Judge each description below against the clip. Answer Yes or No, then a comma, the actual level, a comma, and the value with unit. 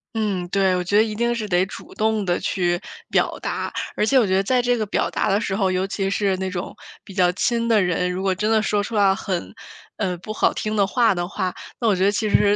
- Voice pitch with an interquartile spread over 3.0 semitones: No, average, 2.7 semitones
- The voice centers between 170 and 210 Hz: Yes, high, 200 Hz